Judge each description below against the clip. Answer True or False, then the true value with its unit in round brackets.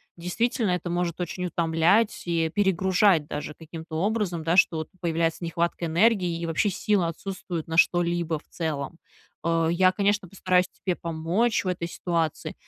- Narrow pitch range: True (2.3 semitones)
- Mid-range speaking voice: True (175 Hz)